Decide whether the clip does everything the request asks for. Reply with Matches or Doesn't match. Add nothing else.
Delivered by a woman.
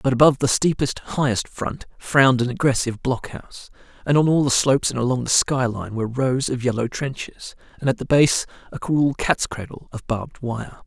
Doesn't match